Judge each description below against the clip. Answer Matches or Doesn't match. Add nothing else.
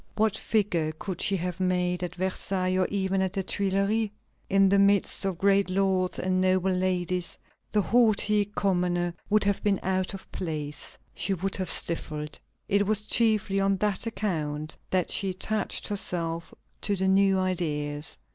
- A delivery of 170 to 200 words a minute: Doesn't match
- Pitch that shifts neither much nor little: Doesn't match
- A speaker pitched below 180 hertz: Doesn't match